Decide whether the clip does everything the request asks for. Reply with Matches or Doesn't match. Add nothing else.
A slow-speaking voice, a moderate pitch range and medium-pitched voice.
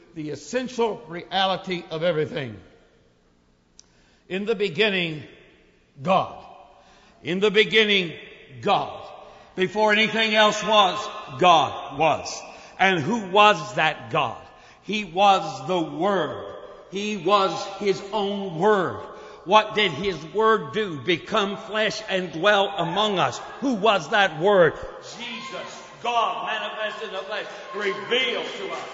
Doesn't match